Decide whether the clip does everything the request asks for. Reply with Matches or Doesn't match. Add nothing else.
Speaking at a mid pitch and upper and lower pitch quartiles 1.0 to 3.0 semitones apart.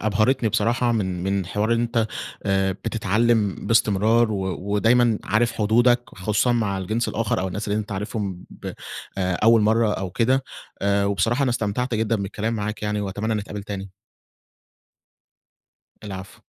Doesn't match